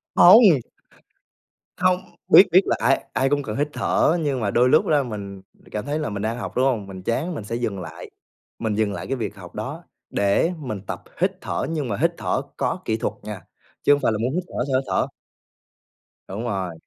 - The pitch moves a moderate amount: No, wide, 5.8 semitones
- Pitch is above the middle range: No, low, 120 Hz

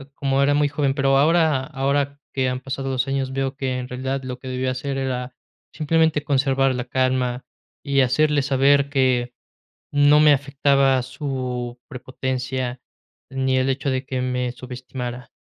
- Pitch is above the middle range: No, low, 135 Hz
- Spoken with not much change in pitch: Yes, narrow, 1.5 semitones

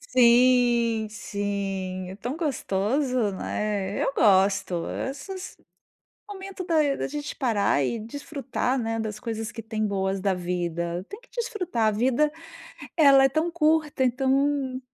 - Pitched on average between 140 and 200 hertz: No, high, 235 Hz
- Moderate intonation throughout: No, wide, 6.0 semitones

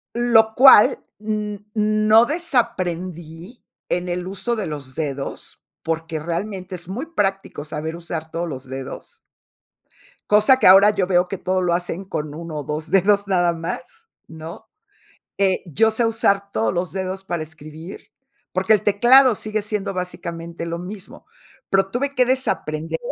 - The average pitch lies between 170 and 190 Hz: Yes, medium, 185 Hz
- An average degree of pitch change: Yes, average, 4.3 semitones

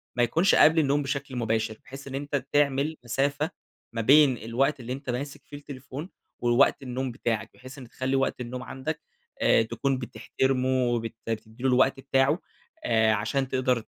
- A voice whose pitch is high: No, low, 130 Hz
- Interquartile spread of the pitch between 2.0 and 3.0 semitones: Yes, narrow, 2.6 semitones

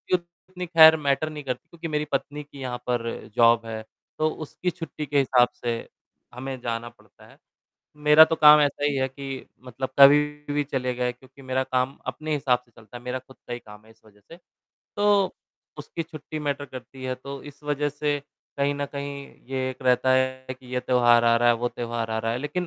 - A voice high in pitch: No, low, 135 Hz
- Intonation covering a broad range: No, average, 3.2 semitones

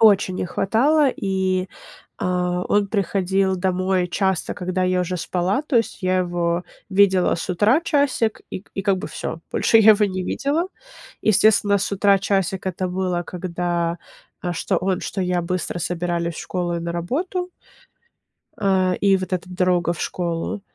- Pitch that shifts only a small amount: Yes, narrow, 2.1 semitones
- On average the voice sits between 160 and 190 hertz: Yes, medium, 185 Hz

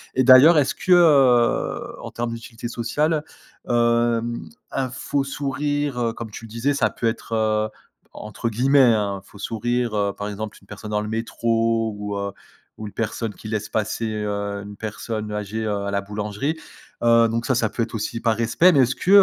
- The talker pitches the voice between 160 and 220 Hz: No, low, 115 Hz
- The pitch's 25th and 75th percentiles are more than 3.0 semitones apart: No, average, 2.7 semitones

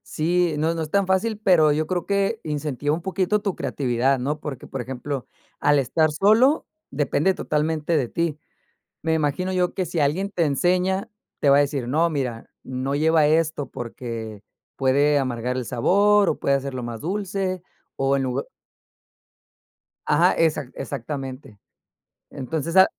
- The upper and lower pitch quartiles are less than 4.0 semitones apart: No, average, 4.9 semitones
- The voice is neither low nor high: Yes, medium, 150 Hz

